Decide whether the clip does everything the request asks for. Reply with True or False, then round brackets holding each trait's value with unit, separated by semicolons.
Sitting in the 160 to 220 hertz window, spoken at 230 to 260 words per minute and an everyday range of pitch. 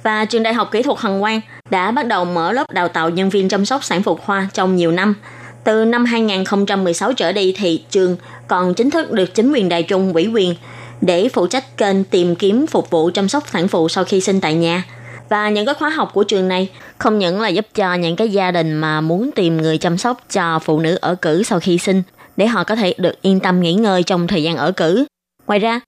True (190 Hz; 245 wpm; 3.8 semitones)